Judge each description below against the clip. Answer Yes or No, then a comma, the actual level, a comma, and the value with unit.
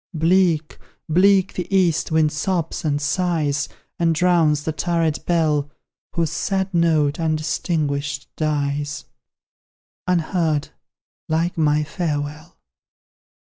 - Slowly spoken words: Yes, slow, 95 wpm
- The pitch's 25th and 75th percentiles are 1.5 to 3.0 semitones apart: Yes, narrow, 2.5 semitones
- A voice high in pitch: No, medium, 160 Hz